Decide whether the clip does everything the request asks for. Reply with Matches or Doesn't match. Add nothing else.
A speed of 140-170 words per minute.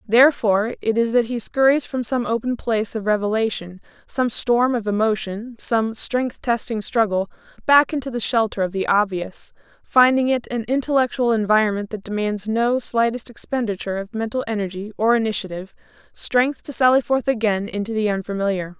Matches